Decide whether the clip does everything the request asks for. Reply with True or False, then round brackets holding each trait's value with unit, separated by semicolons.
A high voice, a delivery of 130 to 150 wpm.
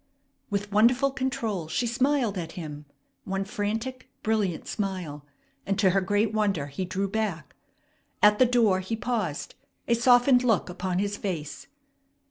True (205 Hz; 145 wpm)